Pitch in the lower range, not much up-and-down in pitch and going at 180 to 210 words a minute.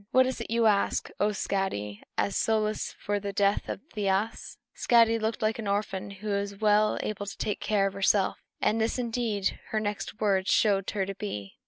No: high, 205 Hz; narrow, 1.7 semitones; average, 195 wpm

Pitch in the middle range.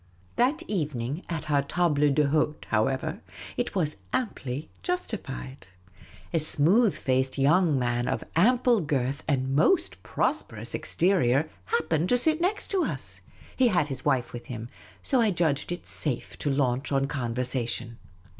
Yes: medium, 150 Hz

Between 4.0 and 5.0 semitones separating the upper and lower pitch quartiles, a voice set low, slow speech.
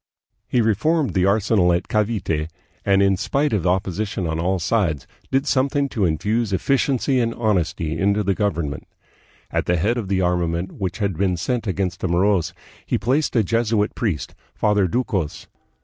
No: average, 4.4 semitones; low, 100 Hz; average, 165 wpm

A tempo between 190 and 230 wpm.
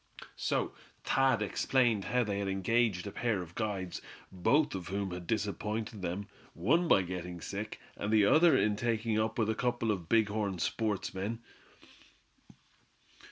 No: average, 155 wpm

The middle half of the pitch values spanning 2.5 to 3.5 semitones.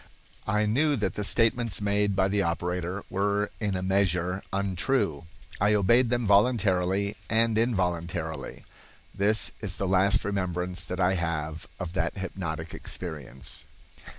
Yes: average, 2.8 semitones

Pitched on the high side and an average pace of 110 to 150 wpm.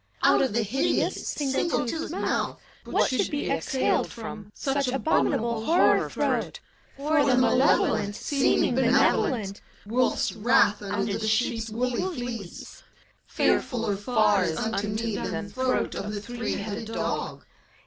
Yes: high, 230 Hz; average, 145 wpm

